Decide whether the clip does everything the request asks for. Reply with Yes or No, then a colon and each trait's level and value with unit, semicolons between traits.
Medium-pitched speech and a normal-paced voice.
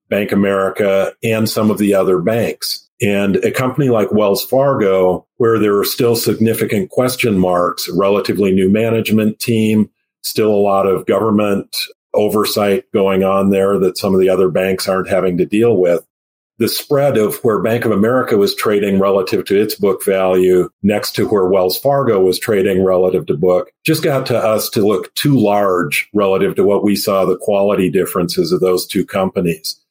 No: low, 100 Hz; average, 180 wpm